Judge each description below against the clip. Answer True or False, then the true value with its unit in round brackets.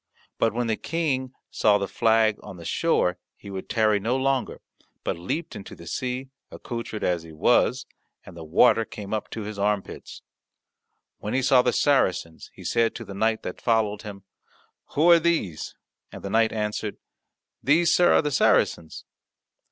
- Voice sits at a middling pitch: False (110 Hz)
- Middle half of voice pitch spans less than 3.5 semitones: False (4.6 semitones)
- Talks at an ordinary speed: True (175 wpm)